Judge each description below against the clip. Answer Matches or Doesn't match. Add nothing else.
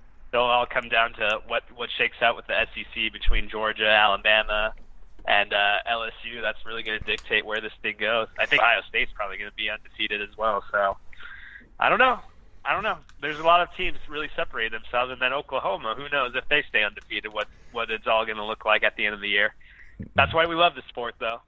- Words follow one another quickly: Matches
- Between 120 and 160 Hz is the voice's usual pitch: Doesn't match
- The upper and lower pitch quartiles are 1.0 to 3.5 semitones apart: Doesn't match